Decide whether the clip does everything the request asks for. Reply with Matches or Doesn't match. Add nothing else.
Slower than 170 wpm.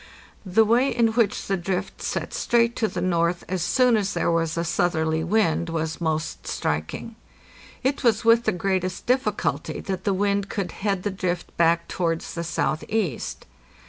Doesn't match